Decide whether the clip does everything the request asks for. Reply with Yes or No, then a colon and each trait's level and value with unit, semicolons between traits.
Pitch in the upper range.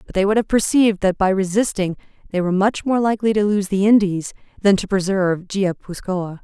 Yes: high, 195 Hz